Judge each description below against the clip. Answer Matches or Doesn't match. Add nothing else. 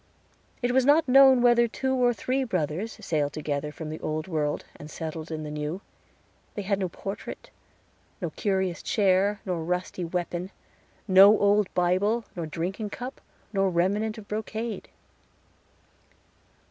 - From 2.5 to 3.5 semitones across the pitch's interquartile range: Doesn't match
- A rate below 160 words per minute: Matches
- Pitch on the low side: Doesn't match